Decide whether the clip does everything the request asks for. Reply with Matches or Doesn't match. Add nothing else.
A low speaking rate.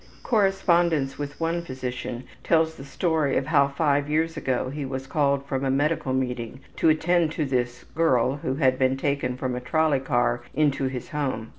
Doesn't match